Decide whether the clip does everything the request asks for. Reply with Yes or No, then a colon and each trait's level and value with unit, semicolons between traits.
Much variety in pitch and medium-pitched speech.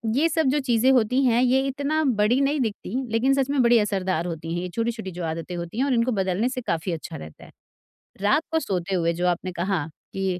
No: wide, 6.6 semitones; high, 220 Hz